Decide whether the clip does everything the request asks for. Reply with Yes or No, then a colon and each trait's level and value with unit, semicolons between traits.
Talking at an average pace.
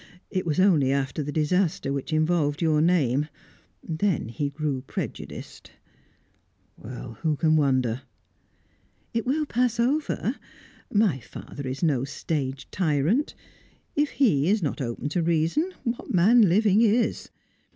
No: slow, 130 wpm